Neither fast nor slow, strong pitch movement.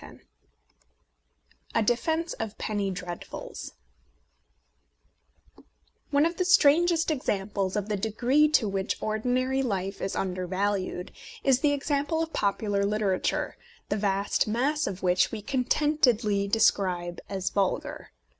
No: slow, 120 wpm; wide, 6.4 semitones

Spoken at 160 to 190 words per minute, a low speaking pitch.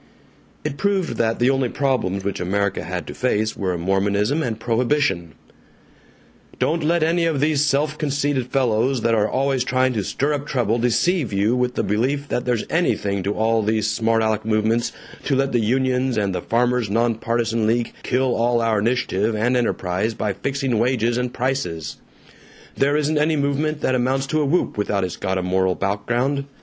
Yes: average, 180 wpm; low, 120 Hz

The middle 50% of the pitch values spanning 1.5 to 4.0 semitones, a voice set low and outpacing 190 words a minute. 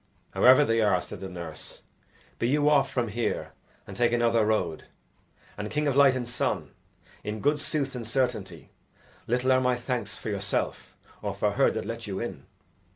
No: average, 3.7 semitones; low, 120 Hz; average, 180 wpm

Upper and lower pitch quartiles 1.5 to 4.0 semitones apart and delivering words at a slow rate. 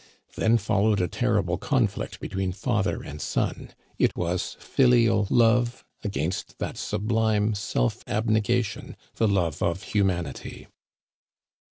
Yes: average, 3.6 semitones; slow, 125 wpm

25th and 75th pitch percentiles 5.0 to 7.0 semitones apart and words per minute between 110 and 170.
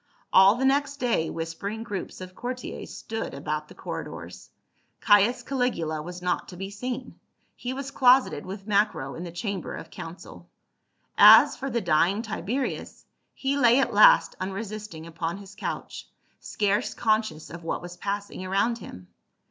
Yes: wide, 5.6 semitones; average, 155 wpm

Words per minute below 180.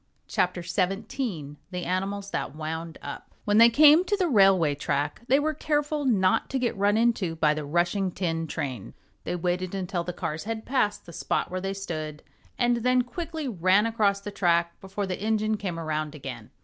No: average, 190 wpm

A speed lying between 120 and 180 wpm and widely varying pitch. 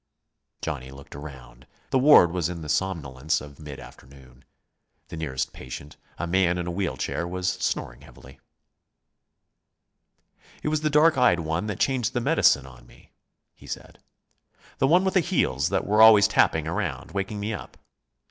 Yes: average, 165 wpm; wide, 7.6 semitones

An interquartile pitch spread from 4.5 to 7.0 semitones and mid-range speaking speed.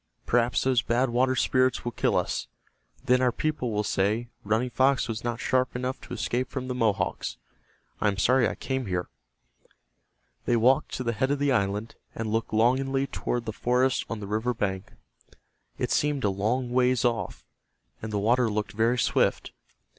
No: average, 2.8 semitones; average, 180 wpm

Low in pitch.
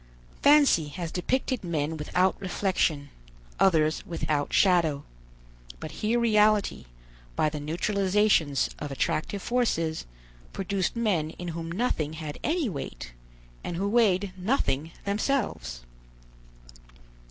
No: medium, 180 Hz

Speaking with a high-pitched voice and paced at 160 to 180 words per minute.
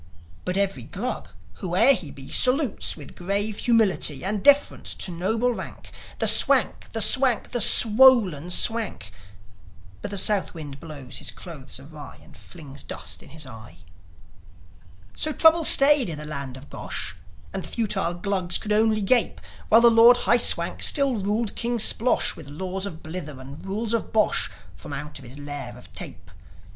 Yes: high, 195 Hz; average, 165 wpm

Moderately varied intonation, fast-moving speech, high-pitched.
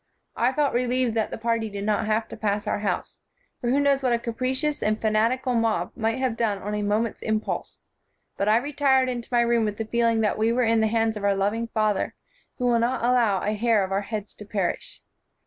No: narrow, 2.3 semitones; fast, 235 wpm; high, 225 Hz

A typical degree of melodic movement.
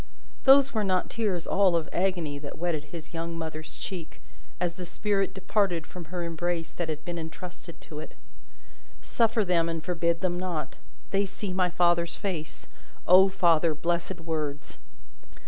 No: narrow, 2.3 semitones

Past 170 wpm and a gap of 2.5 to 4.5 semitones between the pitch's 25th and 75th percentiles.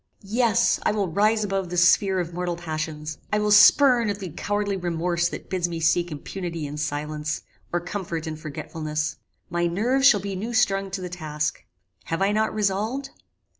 Yes: average, 180 wpm; average, 4.1 semitones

